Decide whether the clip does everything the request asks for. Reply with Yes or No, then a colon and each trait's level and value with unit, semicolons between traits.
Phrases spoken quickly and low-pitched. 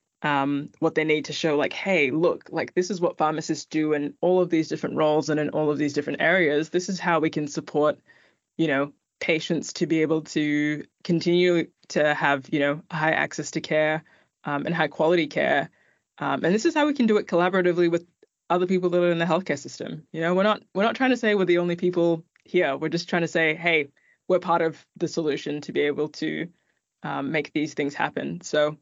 No: fast, 225 wpm; medium, 160 Hz